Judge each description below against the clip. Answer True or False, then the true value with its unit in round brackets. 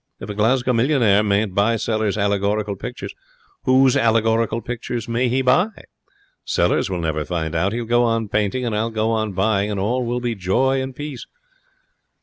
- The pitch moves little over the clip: False (3.2 semitones)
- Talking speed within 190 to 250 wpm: False (175 wpm)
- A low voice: True (110 Hz)